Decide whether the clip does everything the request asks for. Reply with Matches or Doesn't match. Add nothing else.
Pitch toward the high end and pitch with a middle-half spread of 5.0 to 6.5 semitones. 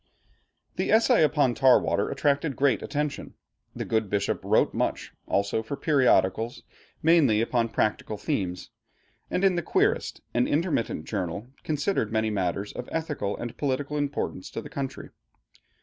Doesn't match